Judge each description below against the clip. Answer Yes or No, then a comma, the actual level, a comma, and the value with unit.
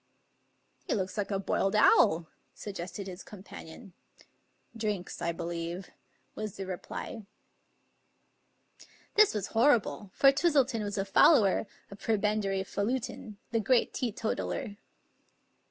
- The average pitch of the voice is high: Yes, high, 205 Hz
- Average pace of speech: No, slow, 120 wpm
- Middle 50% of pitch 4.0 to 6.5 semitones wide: No, average, 2.9 semitones